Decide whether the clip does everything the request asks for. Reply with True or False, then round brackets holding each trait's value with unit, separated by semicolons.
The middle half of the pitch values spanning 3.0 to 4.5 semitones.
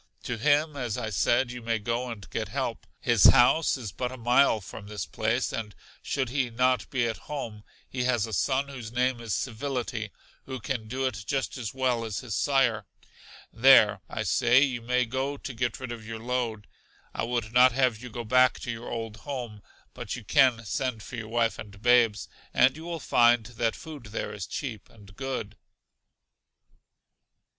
False (2.5 semitones)